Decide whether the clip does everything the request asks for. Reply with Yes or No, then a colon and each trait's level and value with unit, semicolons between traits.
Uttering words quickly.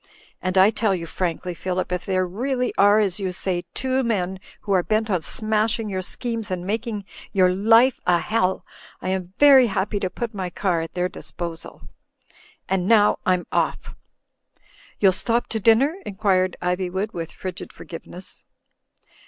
No: average, 170 wpm